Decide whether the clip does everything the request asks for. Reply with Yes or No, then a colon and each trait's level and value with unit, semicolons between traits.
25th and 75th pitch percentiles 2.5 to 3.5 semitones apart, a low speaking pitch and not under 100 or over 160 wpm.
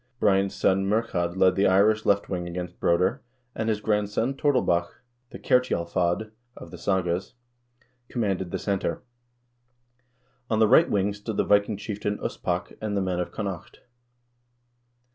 Yes: average, 2.9 semitones; low, 100 Hz; average, 145 wpm